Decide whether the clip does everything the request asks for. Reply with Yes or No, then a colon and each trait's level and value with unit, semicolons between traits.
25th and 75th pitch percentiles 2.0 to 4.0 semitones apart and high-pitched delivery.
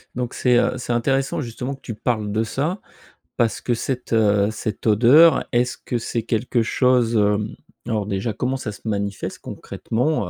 No: average, 2.8 semitones; low, 115 Hz